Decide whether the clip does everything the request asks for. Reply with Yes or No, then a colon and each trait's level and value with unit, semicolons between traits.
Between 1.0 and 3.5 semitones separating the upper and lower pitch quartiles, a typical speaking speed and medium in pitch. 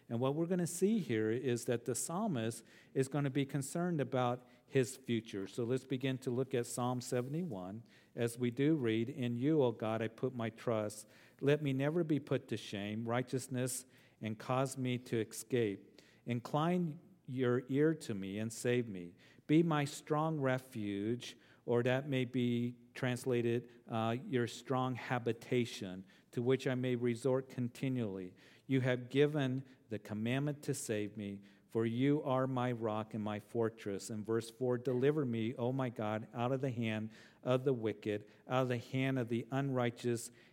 No: average, 2.7 semitones; average, 175 wpm; low, 125 Hz